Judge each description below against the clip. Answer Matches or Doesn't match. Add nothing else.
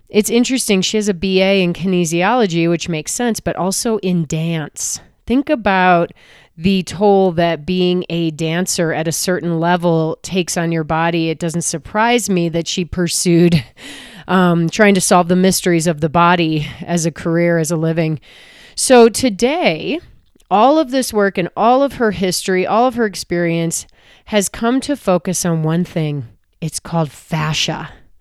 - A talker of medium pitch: Matches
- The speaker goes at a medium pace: Matches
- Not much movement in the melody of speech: Doesn't match